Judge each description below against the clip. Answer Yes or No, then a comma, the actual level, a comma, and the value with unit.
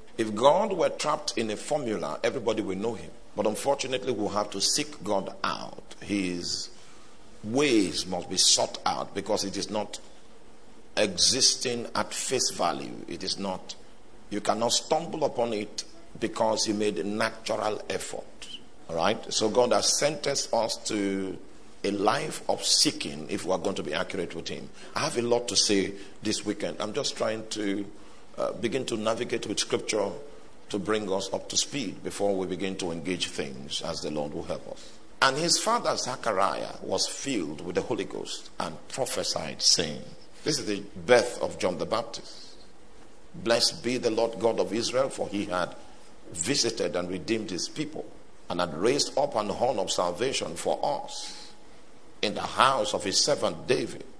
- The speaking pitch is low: Yes, low, 105 Hz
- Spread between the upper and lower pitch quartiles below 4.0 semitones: Yes, average, 3.1 semitones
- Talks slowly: No, average, 175 wpm